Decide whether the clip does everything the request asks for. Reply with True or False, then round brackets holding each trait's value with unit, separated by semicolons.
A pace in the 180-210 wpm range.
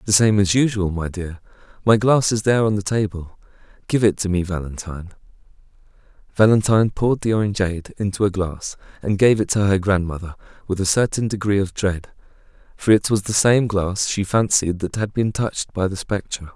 True (185 wpm)